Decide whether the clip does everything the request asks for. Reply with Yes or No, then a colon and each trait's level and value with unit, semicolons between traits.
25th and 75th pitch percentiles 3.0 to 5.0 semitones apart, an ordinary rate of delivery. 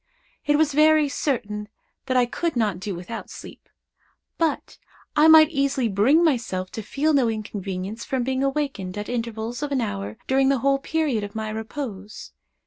No: wide, 5.4 semitones; average, 170 wpm